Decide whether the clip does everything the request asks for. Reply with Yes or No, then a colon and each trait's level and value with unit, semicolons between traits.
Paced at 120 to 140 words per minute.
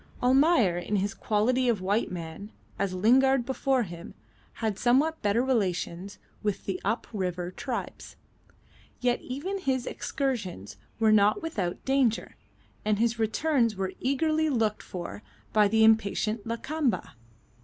Yes: slow, 135 wpm